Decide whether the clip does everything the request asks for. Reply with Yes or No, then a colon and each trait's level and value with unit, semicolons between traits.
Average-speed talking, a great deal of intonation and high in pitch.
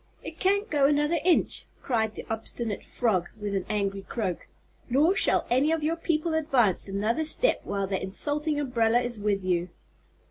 Yes: average, 170 wpm; wide, 7.1 semitones; high, 240 Hz